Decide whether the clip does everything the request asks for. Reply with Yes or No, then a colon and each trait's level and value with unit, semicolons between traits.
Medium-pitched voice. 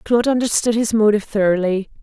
No: high, 215 Hz